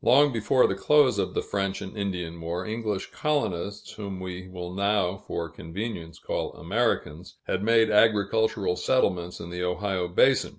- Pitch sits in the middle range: No, low, 100 Hz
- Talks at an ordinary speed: Yes, average, 160 wpm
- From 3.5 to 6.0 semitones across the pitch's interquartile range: Yes, average, 3.8 semitones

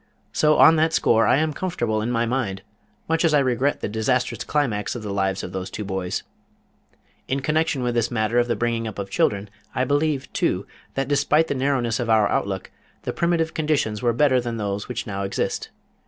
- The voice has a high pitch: No, low, 120 Hz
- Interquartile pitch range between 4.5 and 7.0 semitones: Yes, average, 5.2 semitones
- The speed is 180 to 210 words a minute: Yes, fast, 205 wpm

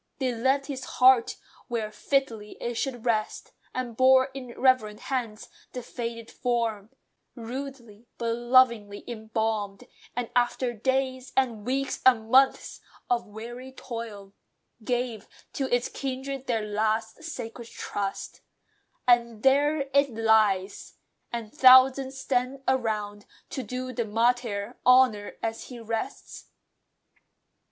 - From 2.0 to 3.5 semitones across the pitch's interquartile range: Yes, average, 2.9 semitones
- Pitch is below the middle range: No, high, 240 Hz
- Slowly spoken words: Yes, slow, 120 wpm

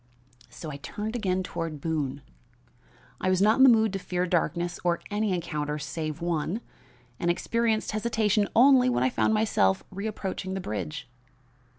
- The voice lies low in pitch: No, medium, 185 Hz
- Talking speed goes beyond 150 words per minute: Yes, average, 160 wpm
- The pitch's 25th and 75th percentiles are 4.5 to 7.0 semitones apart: Yes, average, 5.1 semitones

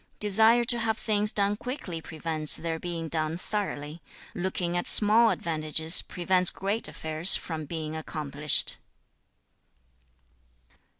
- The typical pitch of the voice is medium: Yes, medium, 175 Hz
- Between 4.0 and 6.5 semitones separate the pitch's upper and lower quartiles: Yes, average, 4.7 semitones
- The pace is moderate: No, slow, 115 wpm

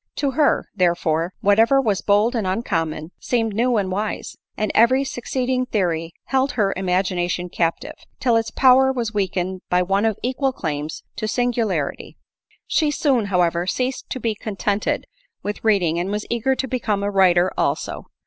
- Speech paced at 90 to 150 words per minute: No, average, 165 wpm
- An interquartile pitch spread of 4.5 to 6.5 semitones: Yes, average, 5.3 semitones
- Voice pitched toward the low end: No, high, 210 Hz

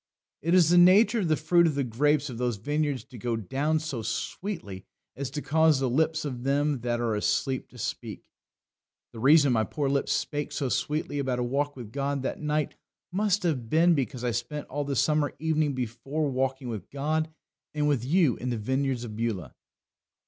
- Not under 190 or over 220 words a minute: Yes, average, 200 wpm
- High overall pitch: No, medium, 140 Hz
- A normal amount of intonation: Yes, average, 4.0 semitones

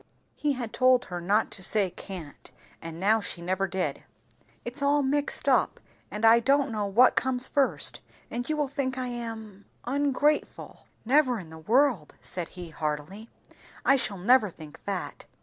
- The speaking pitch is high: Yes, high, 225 Hz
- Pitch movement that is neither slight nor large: No, wide, 5.8 semitones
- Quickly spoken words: No, average, 165 wpm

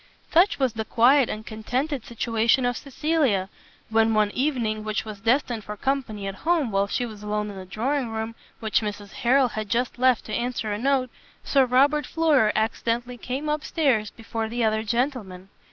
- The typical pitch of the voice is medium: No, high, 230 Hz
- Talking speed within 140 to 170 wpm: No, average, 185 wpm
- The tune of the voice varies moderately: Yes, average, 3.6 semitones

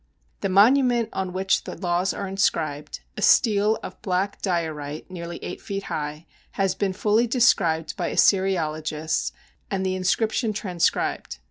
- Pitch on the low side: No, high, 190 Hz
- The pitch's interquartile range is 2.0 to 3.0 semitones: No, average, 3.7 semitones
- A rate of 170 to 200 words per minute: No, average, 140 wpm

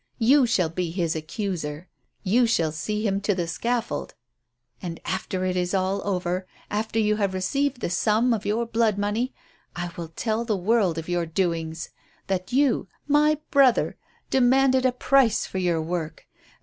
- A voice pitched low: No, high, 200 Hz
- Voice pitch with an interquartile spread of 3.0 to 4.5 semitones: No, average, 5.0 semitones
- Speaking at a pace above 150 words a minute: Yes, average, 160 wpm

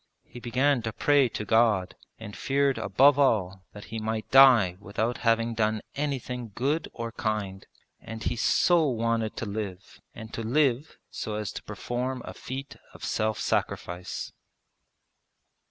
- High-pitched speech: No, low, 115 Hz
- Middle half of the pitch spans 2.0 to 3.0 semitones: No, average, 3.4 semitones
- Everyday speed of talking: Yes, average, 150 wpm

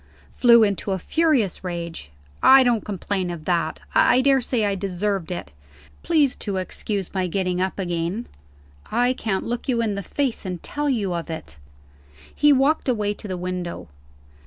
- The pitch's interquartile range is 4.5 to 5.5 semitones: Yes, average, 5.2 semitones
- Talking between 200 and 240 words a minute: No, average, 165 wpm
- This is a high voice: Yes, high, 200 Hz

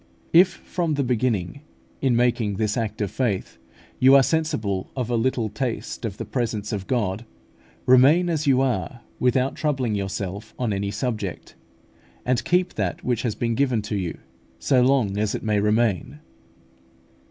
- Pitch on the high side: No, low, 120 Hz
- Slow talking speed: No, average, 160 wpm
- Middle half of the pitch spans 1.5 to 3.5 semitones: No, average, 4.0 semitones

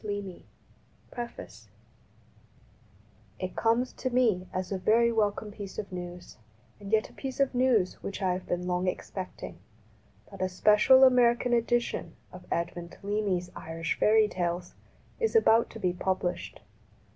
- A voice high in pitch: Yes, high, 205 Hz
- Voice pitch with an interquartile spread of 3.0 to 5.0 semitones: Yes, average, 4.4 semitones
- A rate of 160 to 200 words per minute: No, average, 145 wpm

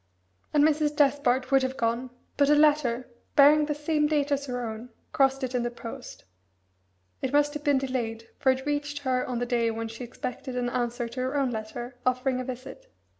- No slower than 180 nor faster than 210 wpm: Yes, fast, 205 wpm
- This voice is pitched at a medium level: No, very high, 260 Hz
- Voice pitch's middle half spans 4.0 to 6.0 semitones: No, average, 3.0 semitones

